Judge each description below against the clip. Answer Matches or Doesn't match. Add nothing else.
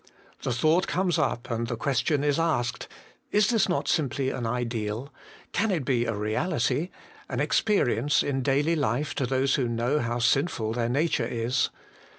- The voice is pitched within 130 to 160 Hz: Matches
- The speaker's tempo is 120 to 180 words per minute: Matches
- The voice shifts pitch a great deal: Doesn't match